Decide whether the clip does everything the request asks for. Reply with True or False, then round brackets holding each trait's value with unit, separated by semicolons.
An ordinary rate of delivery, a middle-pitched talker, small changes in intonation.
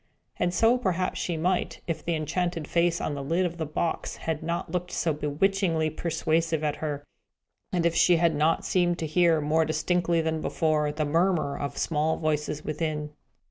True (180 wpm; 160 Hz; 2.2 semitones)